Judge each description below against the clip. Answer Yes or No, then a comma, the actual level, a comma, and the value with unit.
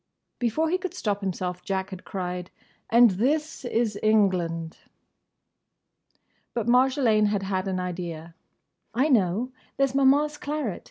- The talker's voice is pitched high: Yes, high, 215 Hz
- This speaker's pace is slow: Yes, slow, 130 wpm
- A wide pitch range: Yes, wide, 6.2 semitones